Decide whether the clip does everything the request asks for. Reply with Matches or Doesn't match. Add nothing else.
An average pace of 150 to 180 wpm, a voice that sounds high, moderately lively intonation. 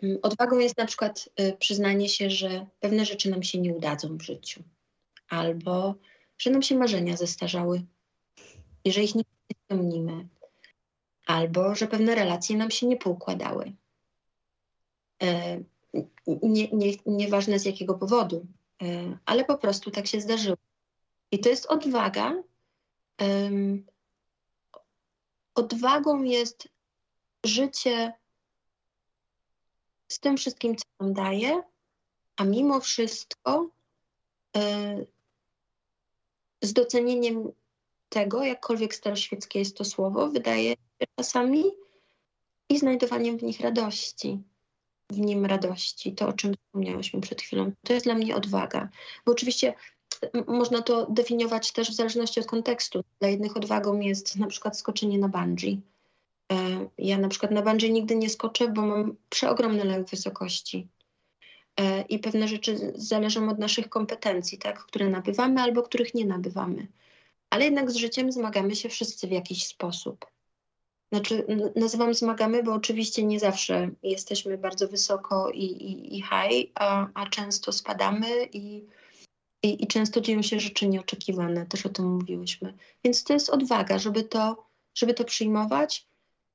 Doesn't match